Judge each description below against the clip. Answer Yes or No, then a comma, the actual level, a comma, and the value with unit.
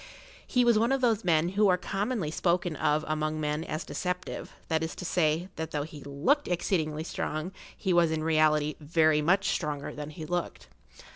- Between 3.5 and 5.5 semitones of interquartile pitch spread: No, average, 3.0 semitones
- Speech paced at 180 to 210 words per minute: Yes, average, 190 wpm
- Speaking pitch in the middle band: Yes, medium, 160 Hz